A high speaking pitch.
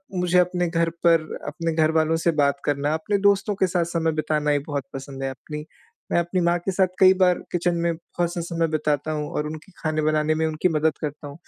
No: medium, 160 Hz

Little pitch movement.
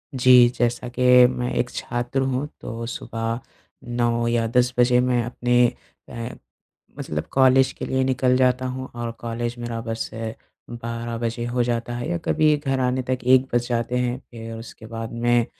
Yes: narrow, 1.4 semitones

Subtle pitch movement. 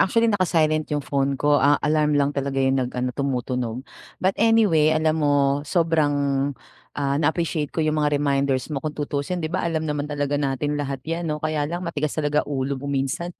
Yes: narrow, 2.2 semitones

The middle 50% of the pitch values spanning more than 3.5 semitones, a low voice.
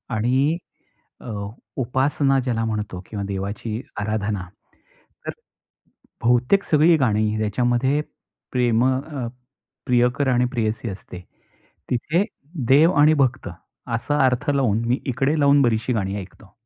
Yes: average, 4.1 semitones; low, 125 Hz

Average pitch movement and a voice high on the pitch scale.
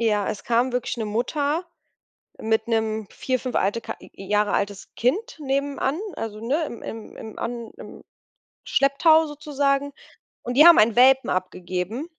Yes: average, 4.5 semitones; high, 245 Hz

